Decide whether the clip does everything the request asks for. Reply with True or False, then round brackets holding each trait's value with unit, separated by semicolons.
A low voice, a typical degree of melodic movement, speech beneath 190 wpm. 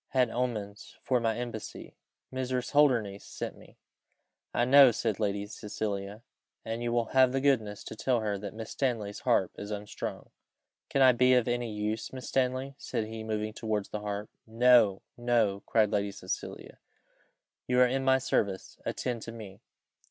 True (115 Hz; 3.2 semitones; 165 wpm)